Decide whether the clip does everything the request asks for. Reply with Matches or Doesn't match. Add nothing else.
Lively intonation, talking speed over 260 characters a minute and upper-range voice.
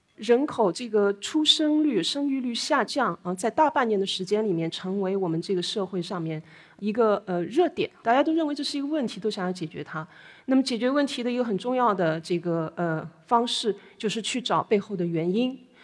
Matches